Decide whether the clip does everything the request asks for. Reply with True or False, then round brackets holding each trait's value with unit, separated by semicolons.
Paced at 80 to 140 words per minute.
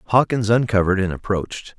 True (135 wpm)